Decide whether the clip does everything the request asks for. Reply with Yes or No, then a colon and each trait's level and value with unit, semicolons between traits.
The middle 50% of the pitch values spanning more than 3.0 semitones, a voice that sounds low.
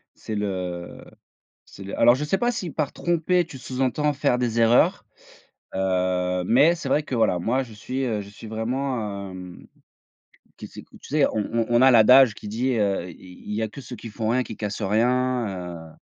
Yes: average, 4.8 semitones; low, 115 Hz